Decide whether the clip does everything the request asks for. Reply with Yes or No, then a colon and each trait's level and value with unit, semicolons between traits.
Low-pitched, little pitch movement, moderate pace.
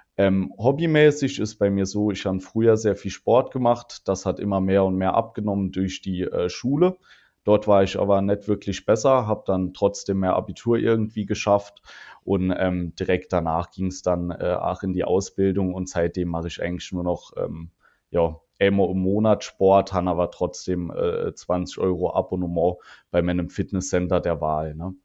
Yes: very low, 95 Hz; narrow, 2.3 semitones; average, 180 wpm